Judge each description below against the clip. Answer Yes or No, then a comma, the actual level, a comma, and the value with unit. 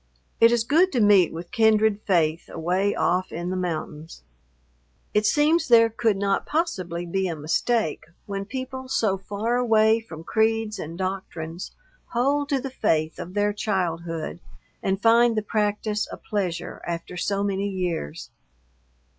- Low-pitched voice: No, high, 200 Hz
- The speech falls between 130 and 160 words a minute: Yes, average, 150 wpm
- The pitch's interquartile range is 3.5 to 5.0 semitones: Yes, average, 4.6 semitones